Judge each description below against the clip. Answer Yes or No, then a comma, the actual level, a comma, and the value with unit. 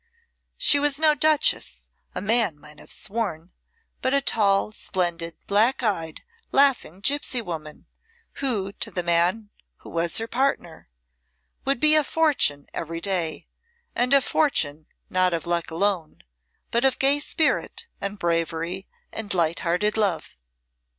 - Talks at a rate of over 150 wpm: No, average, 140 wpm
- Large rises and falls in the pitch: Yes, wide, 7.9 semitones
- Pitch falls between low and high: No, high, 200 Hz